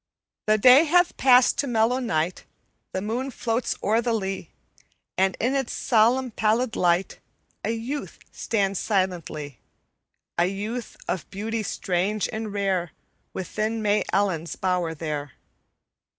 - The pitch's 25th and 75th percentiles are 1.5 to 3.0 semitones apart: No, average, 4.1 semitones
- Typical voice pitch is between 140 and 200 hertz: No, high, 210 Hz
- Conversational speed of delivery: No, slow, 130 wpm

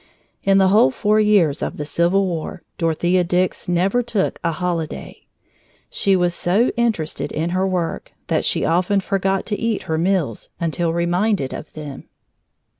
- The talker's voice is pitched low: No, medium, 180 Hz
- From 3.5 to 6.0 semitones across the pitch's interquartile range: No, average, 2.9 semitones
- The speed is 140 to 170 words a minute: Yes, average, 160 wpm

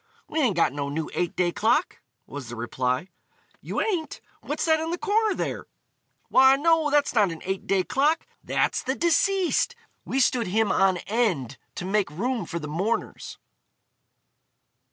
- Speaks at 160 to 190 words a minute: Yes, average, 165 wpm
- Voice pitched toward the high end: Yes, high, 220 Hz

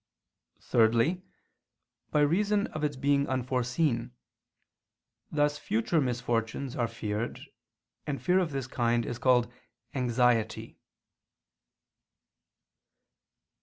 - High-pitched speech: No, low, 125 Hz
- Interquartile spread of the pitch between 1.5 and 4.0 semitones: Yes, average, 3.7 semitones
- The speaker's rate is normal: No, slow, 90 wpm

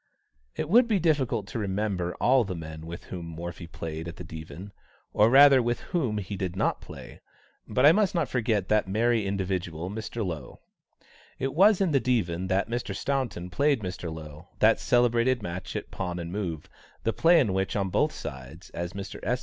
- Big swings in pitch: Yes, wide, 6.1 semitones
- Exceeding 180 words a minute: Yes, average, 190 wpm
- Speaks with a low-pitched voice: Yes, low, 100 Hz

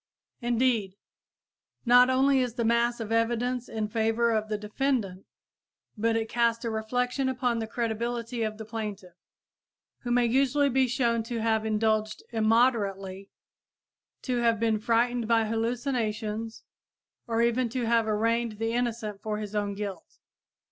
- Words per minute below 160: Yes, average, 145 wpm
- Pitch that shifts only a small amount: Yes, narrow, 1.9 semitones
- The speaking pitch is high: Yes, high, 230 Hz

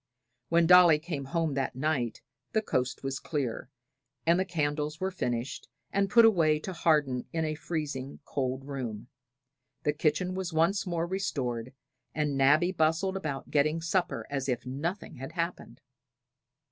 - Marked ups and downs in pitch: No, average, 4.2 semitones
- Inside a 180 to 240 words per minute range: No, average, 150 wpm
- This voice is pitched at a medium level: Yes, medium, 155 Hz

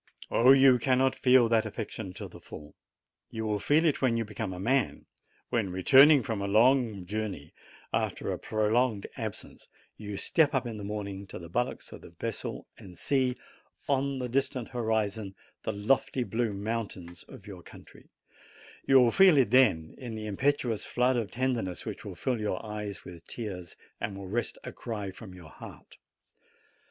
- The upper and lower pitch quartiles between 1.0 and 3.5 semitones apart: No, average, 4.3 semitones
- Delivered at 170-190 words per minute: Yes, average, 175 wpm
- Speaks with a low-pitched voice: Yes, low, 110 Hz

